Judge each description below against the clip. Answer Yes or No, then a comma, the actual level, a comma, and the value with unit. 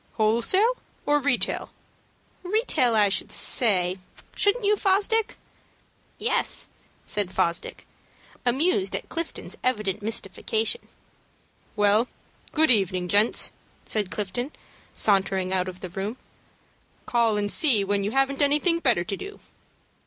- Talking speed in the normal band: No, slow, 120 wpm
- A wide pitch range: Yes, wide, 7.0 semitones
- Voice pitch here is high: Yes, high, 220 Hz